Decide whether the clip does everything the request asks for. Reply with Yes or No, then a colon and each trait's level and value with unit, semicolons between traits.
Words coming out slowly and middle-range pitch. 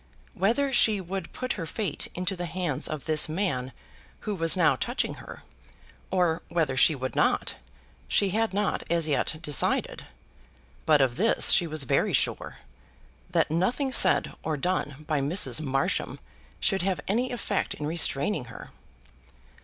No: average, 155 wpm; medium, 170 Hz